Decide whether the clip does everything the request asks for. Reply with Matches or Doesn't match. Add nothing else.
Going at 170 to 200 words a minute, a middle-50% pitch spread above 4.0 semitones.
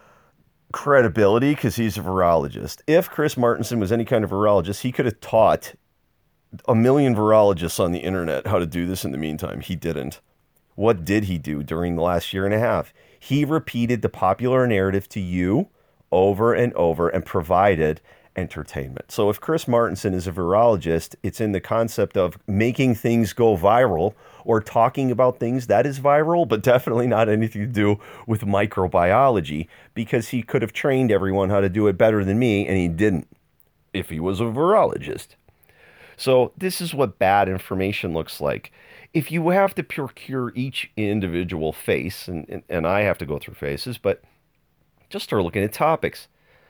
Matches